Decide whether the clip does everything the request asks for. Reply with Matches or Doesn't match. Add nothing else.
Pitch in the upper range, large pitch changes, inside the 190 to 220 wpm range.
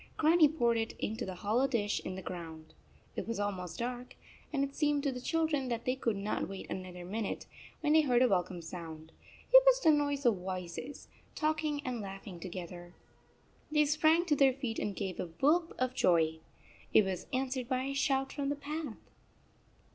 Matches